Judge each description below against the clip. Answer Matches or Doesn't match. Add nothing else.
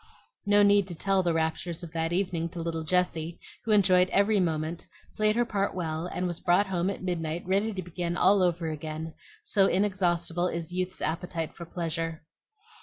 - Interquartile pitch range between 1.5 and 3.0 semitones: Matches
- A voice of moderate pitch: Matches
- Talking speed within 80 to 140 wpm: Doesn't match